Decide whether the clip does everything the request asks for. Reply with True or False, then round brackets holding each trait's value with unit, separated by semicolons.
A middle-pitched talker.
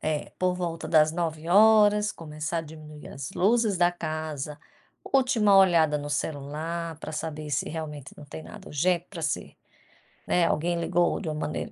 True (165 Hz)